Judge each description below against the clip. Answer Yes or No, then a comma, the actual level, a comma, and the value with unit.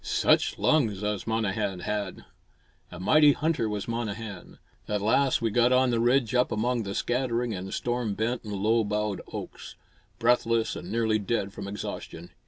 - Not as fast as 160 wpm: No, average, 165 wpm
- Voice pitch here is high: No, low, 110 Hz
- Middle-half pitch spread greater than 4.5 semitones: No, average, 3.0 semitones